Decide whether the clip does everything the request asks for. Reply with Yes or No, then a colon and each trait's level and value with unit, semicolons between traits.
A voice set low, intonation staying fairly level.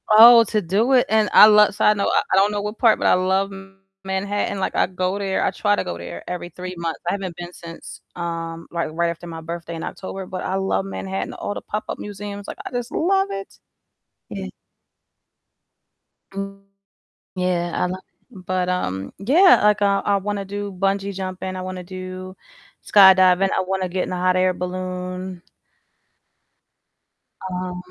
No: high, 190 Hz; narrow, 1.9 semitones